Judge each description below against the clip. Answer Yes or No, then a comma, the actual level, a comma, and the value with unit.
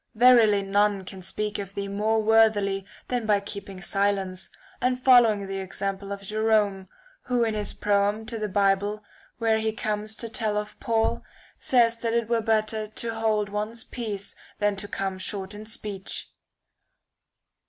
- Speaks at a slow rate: No, average, 160 wpm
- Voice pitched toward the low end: No, high, 210 Hz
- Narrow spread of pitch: Yes, narrow, 2.0 semitones